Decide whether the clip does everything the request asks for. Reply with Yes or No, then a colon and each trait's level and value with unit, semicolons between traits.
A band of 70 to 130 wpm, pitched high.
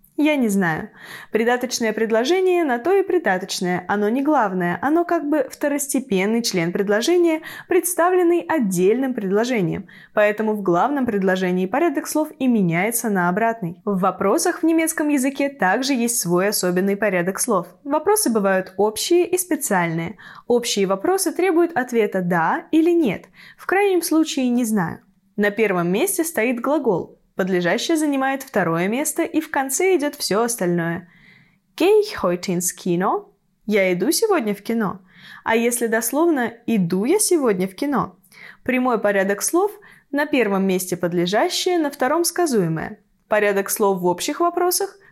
No: average, 140 wpm; high, 225 Hz